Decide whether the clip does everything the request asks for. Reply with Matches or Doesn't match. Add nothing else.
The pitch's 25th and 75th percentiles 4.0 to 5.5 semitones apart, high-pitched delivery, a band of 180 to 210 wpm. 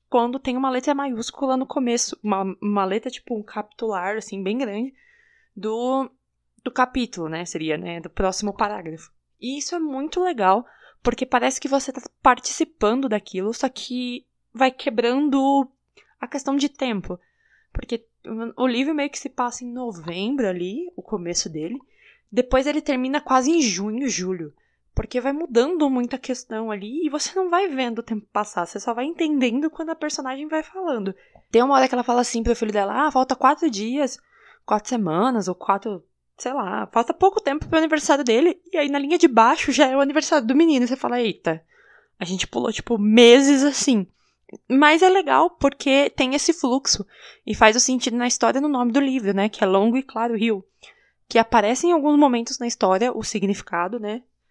Matches